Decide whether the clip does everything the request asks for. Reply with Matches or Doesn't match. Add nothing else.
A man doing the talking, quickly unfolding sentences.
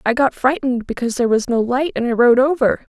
Doesn't match